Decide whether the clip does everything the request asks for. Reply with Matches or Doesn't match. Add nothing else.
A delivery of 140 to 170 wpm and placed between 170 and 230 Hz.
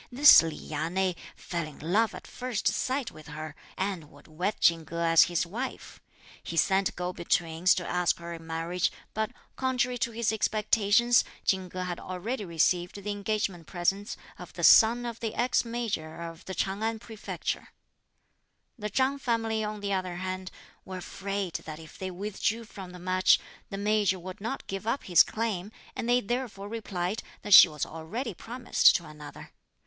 Doesn't match